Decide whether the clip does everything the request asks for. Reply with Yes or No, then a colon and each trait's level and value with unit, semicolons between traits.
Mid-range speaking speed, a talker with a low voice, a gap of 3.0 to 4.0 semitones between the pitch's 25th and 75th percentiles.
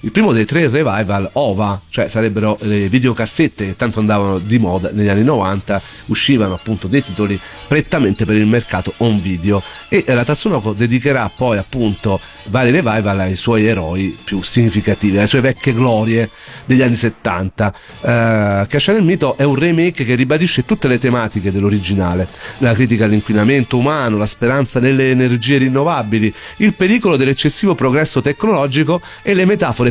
No: average, 160 wpm; low, 115 Hz; average, 4.7 semitones